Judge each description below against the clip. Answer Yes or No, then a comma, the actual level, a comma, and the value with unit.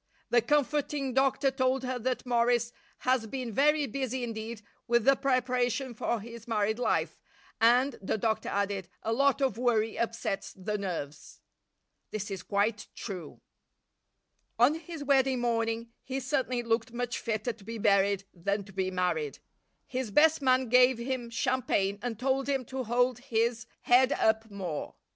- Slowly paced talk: No, average, 155 wpm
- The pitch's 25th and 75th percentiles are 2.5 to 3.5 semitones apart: Yes, average, 3.2 semitones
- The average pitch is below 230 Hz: No, high, 235 Hz